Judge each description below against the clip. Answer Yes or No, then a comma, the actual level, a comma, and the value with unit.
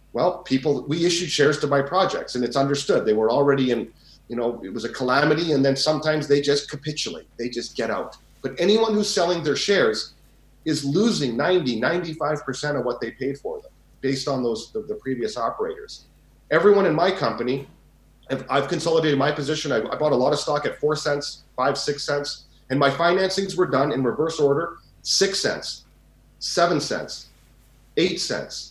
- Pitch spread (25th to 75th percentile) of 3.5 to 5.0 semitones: Yes, average, 4.1 semitones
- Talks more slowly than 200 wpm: Yes, average, 190 wpm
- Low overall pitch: No, medium, 145 Hz